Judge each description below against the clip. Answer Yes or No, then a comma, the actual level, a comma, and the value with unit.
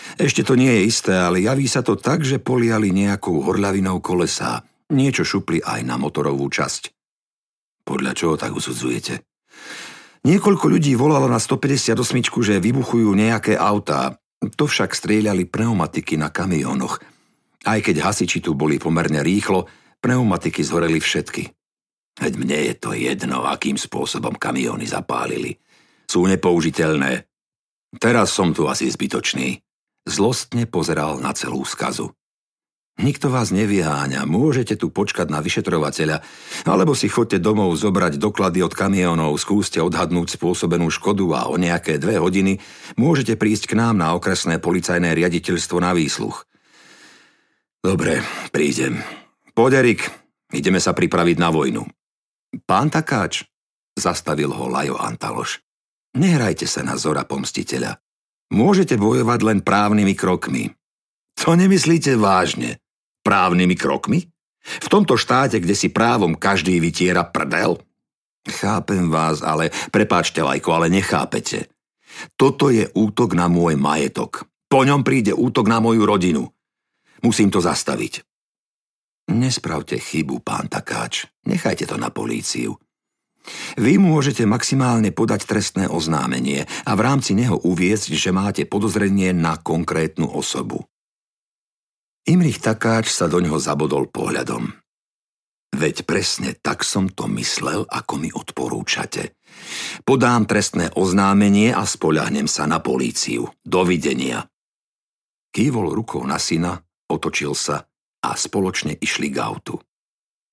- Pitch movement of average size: Yes, average, 5.0 semitones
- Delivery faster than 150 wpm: No, average, 125 wpm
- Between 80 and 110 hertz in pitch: Yes, low, 100 Hz